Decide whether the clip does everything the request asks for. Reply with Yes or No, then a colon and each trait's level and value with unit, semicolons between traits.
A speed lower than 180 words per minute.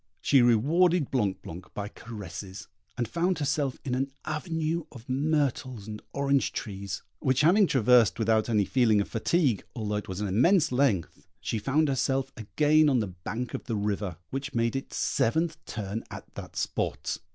Yes: average, 170 wpm